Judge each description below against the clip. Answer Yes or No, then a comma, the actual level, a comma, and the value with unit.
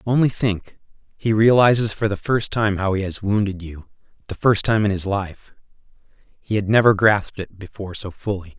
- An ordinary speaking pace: Yes, average, 190 wpm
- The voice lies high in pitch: No, low, 100 Hz